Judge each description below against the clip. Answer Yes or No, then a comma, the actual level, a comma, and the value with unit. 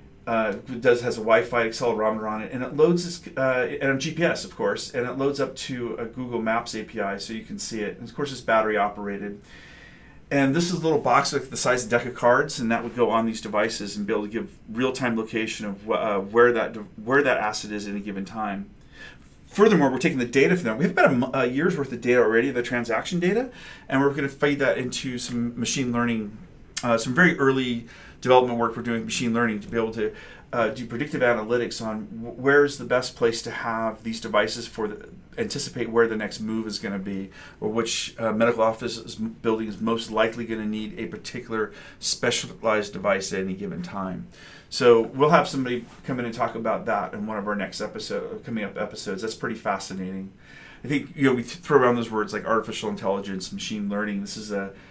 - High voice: No, low, 115 Hz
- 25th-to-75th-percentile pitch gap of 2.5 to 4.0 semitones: Yes, average, 2.8 semitones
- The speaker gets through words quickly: Yes, fast, 230 wpm